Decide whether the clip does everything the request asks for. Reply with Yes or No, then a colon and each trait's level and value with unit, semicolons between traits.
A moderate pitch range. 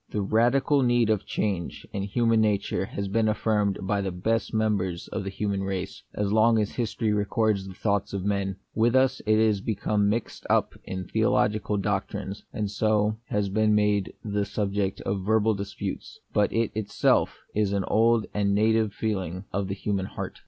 No: narrow, 1.8 semitones